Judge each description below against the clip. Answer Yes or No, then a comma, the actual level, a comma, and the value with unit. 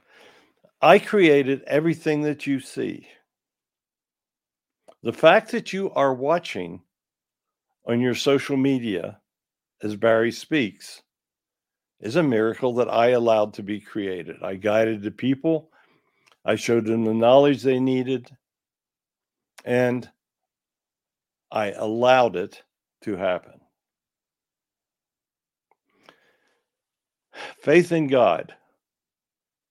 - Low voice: Yes, low, 125 Hz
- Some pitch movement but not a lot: Yes, average, 3.9 semitones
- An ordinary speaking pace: No, slow, 95 wpm